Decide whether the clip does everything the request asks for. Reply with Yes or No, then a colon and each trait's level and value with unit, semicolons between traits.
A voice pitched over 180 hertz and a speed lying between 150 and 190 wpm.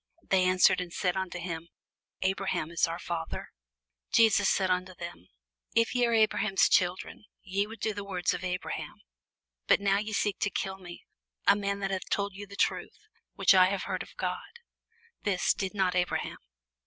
Yes: high, 190 Hz; average, 180 wpm